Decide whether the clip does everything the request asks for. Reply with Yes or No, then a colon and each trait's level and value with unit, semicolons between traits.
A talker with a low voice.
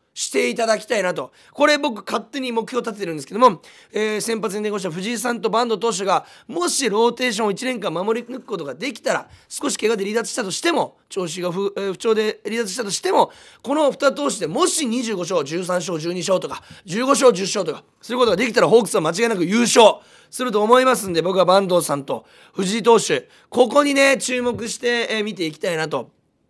No: high, 230 Hz